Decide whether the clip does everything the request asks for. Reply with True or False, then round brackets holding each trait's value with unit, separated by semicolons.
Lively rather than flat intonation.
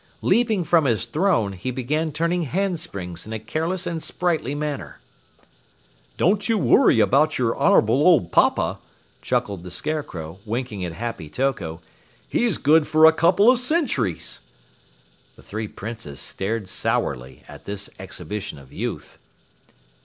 True (8.7 semitones)